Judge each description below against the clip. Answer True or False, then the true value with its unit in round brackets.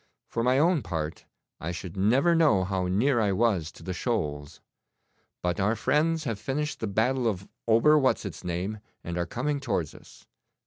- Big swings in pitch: True (6.7 semitones)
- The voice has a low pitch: True (110 Hz)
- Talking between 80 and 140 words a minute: False (180 wpm)